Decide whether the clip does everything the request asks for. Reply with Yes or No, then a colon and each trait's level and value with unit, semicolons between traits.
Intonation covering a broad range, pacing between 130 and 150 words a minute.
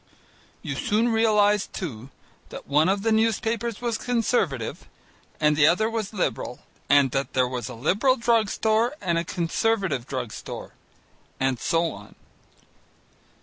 Yes: wide, 8.4 semitones; average, 145 wpm